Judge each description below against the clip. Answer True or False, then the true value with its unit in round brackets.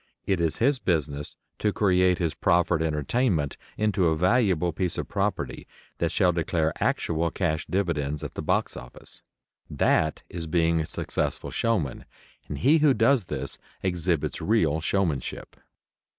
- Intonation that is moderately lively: True (4.1 semitones)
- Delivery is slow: False (145 wpm)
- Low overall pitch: True (85 Hz)